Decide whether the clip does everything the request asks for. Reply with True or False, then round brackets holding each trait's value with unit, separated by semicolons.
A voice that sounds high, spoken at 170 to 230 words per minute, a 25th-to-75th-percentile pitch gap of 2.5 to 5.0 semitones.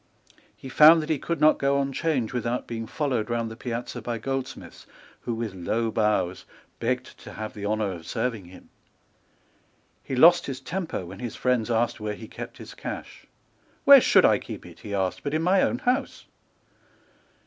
False (120 Hz; 185 wpm; 4.3 semitones)